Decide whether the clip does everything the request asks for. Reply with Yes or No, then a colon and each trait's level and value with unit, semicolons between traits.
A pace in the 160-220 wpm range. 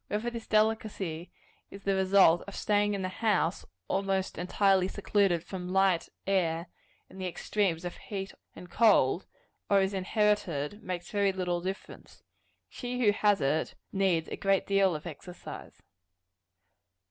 No: average, 145 wpm